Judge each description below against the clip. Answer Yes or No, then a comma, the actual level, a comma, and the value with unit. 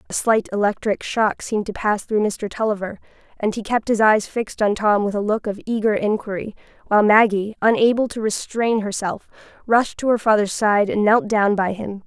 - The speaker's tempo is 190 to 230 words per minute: Yes, average, 200 wpm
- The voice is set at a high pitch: Yes, high, 210 Hz